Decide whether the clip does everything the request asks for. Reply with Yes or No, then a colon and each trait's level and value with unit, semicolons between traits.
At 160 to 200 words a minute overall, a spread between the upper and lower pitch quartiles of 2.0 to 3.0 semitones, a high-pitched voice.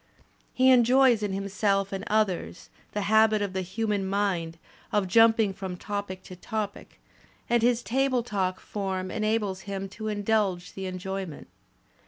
No: average, 145 wpm; narrow, 2.6 semitones; high, 200 Hz